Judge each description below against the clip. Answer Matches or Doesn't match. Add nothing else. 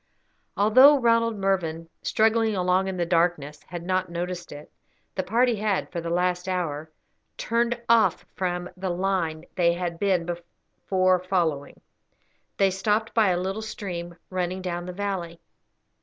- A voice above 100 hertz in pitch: Matches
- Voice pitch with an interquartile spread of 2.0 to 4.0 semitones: Matches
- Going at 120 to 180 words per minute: Matches